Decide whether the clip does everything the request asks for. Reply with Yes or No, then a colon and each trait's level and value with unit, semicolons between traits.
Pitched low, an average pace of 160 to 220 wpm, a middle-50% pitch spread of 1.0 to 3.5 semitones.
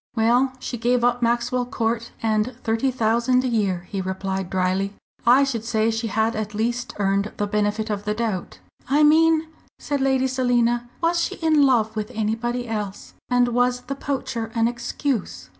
No: high, 235 Hz; average, 175 wpm; average, 2.8 semitones